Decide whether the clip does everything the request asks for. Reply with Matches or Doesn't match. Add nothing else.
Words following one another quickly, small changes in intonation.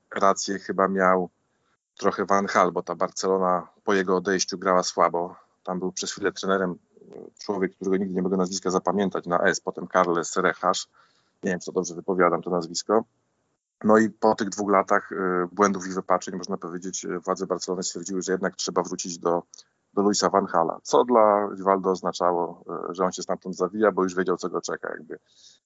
Matches